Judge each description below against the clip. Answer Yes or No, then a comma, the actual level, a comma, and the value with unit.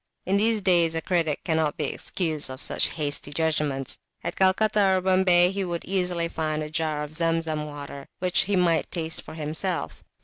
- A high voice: No, medium, 165 Hz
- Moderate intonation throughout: Yes, average, 3.2 semitones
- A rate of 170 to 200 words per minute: Yes, average, 180 wpm